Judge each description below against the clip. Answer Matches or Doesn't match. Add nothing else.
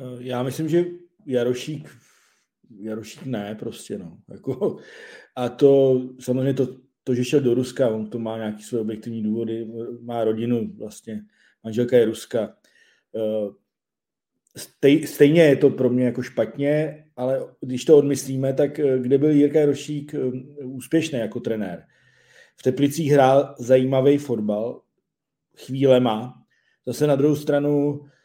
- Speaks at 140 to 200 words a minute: Doesn't match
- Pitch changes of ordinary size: Matches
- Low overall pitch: Matches